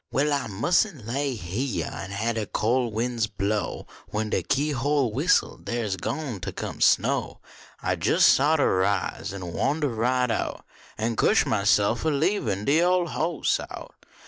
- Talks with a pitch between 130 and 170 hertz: No, low, 120 Hz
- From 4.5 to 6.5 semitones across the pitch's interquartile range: Yes, average, 5.3 semitones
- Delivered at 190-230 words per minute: No, average, 170 wpm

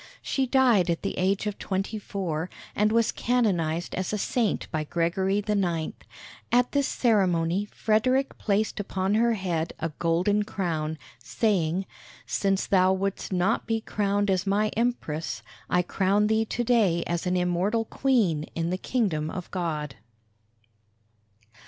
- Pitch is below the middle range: No, high, 195 Hz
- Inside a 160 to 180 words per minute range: No, average, 145 wpm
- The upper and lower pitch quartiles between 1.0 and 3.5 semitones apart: No, average, 4.0 semitones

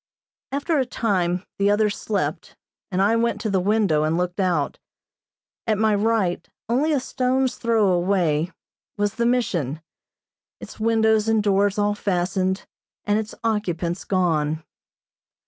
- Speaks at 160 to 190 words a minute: No, average, 140 wpm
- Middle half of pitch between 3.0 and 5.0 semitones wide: Yes, average, 3.8 semitones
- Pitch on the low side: No, high, 205 Hz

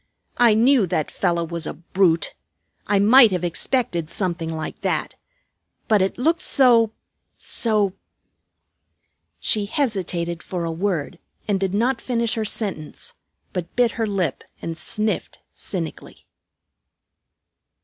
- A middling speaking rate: No, slow, 130 wpm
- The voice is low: No, high, 195 Hz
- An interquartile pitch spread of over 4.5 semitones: Yes, average, 5.0 semitones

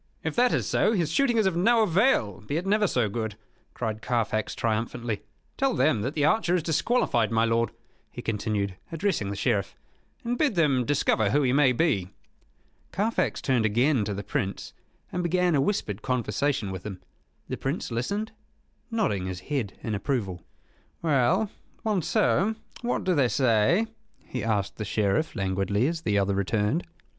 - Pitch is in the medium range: No, low, 125 Hz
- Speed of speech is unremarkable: Yes, average, 170 wpm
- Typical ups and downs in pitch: No, wide, 8.9 semitones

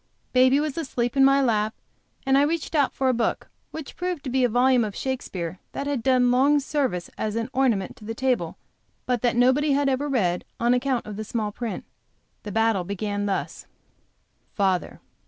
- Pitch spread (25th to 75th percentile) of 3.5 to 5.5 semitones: Yes, average, 4.1 semitones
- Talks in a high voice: Yes, very high, 250 Hz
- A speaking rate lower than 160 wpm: No, average, 195 wpm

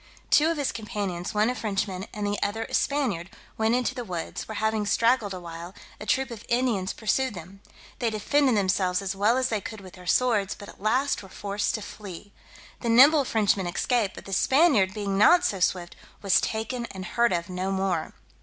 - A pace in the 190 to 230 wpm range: Yes, average, 200 wpm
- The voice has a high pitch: Yes, high, 210 Hz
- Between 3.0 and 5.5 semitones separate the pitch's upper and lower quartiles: Yes, average, 3.9 semitones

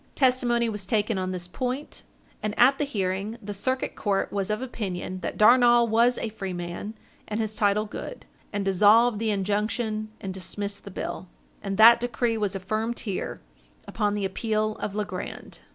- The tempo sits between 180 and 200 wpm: No, average, 170 wpm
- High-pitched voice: Yes, high, 215 Hz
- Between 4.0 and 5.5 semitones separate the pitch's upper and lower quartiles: No, average, 3.0 semitones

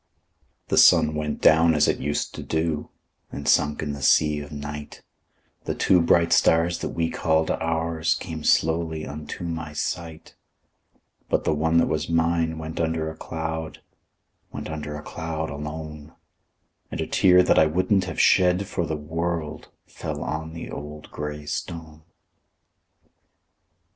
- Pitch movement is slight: Yes, narrow, 1.5 semitones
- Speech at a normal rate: Yes, average, 155 wpm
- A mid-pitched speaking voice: No, very low, 80 Hz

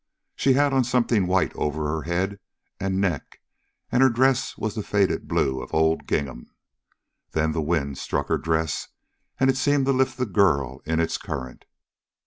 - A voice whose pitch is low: Yes, very low, 95 Hz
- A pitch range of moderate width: No, wide, 8.2 semitones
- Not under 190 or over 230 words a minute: No, average, 175 wpm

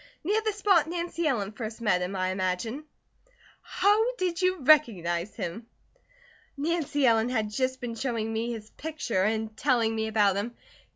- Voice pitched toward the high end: Yes, high, 235 Hz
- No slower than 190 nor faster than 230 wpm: No, average, 160 wpm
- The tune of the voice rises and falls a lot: Yes, wide, 6.4 semitones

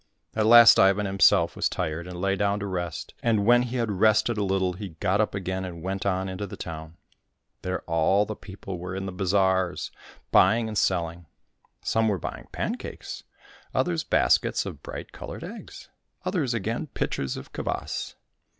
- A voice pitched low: Yes, very low, 95 Hz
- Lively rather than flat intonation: No, average, 2.8 semitones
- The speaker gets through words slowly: No, average, 175 wpm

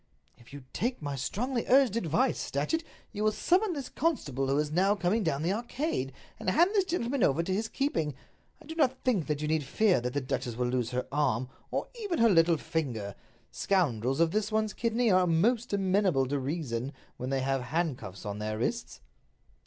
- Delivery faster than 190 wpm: Yes, average, 200 wpm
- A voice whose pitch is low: No, medium, 170 Hz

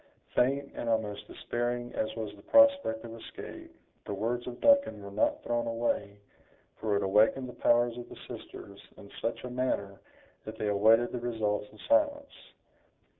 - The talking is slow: No, average, 170 wpm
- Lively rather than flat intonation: No, average, 2.7 semitones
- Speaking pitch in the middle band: No, low, 115 Hz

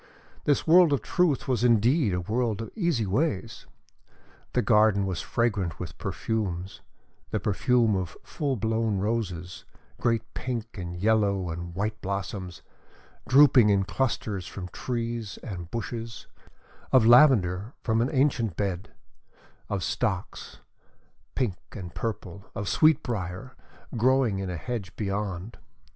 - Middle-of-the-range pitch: No, low, 110 Hz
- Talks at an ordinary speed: No, slow, 125 wpm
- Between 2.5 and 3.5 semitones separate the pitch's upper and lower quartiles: No, average, 4.2 semitones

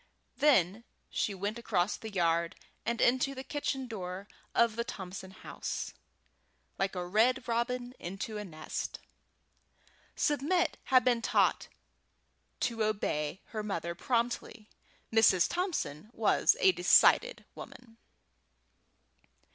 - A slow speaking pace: Yes, slow, 115 wpm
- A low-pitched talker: No, high, 220 Hz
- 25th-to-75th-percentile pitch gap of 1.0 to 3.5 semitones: No, average, 4.9 semitones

